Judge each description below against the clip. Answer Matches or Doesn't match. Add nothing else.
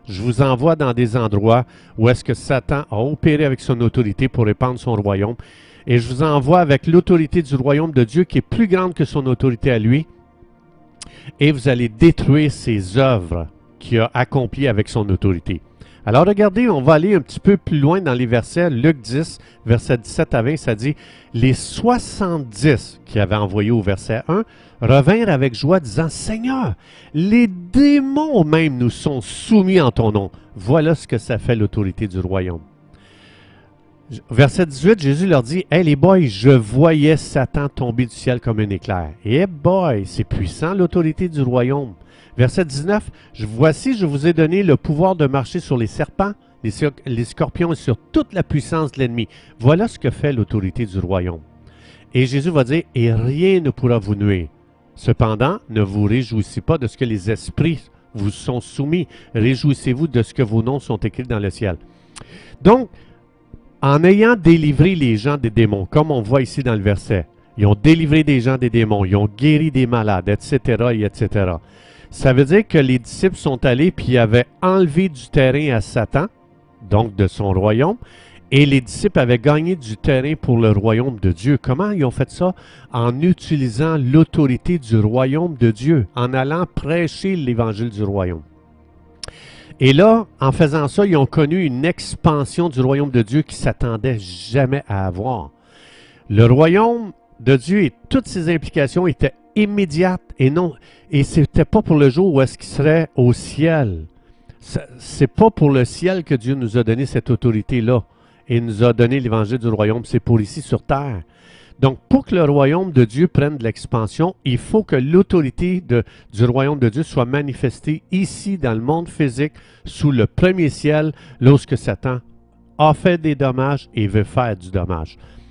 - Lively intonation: Matches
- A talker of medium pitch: Doesn't match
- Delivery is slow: Doesn't match